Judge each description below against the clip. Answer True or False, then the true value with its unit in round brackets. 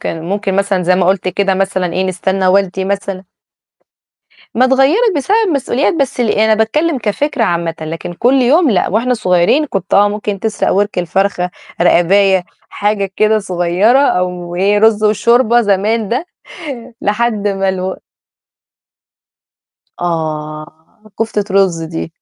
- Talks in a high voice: True (200 Hz)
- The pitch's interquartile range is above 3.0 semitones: True (3.6 semitones)